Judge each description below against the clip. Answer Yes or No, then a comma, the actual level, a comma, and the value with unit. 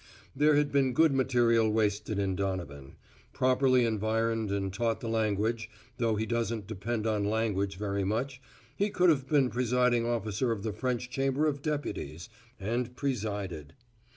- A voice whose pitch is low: Yes, low, 115 Hz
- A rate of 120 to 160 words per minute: Yes, average, 155 wpm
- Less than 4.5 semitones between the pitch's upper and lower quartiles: Yes, average, 3.8 semitones